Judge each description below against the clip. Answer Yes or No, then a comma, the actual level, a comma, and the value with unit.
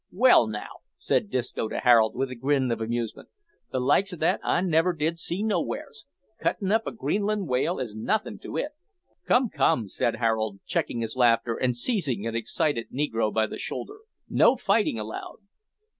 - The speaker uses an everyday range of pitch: No, wide, 7.7 semitones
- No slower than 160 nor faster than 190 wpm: Yes, average, 175 wpm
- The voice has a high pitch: No, low, 125 Hz